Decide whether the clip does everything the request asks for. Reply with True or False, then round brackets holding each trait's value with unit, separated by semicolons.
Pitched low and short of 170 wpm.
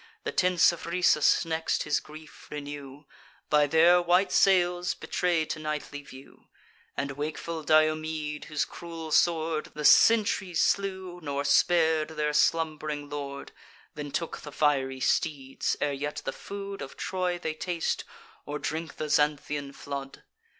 False (155 Hz; 140 wpm)